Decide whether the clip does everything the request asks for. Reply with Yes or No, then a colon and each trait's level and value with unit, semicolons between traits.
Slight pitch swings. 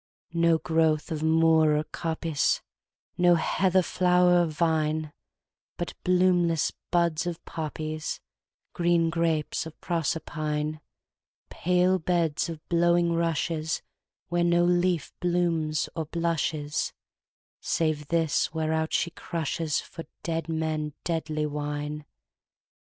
Yes: narrow, 1.9 semitones